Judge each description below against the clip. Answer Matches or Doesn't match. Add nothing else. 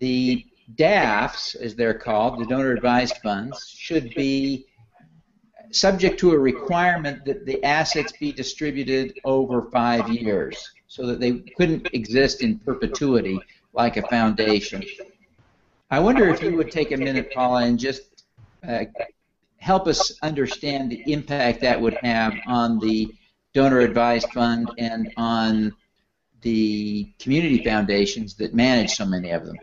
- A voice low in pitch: Matches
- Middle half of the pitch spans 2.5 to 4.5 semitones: Matches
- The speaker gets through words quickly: Doesn't match